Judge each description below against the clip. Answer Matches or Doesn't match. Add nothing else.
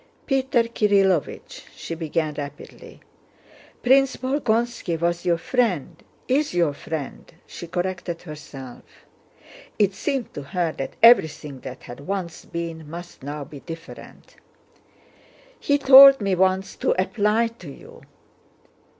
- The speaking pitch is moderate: Matches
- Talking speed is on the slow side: Matches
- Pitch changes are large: Matches